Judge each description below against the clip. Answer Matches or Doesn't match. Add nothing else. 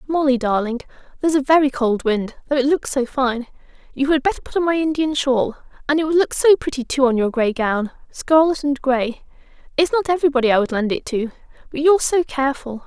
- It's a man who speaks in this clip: Doesn't match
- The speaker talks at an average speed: Doesn't match